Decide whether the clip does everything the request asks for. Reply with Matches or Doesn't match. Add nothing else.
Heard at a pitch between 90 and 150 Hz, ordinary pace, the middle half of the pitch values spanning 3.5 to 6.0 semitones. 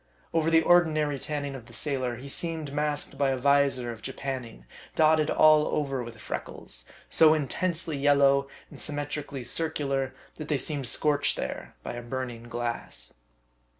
Doesn't match